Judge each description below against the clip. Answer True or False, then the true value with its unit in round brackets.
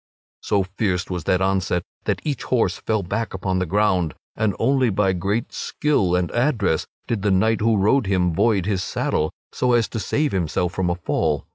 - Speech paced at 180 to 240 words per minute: True (190 wpm)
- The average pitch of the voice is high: False (95 Hz)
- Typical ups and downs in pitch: True (3.8 semitones)